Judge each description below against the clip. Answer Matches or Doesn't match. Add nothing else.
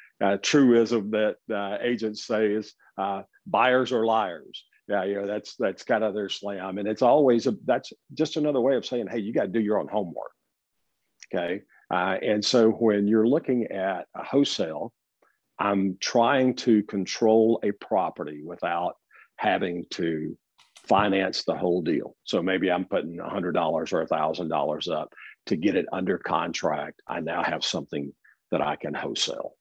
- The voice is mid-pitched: Doesn't match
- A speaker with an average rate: Matches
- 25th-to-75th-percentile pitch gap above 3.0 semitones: Doesn't match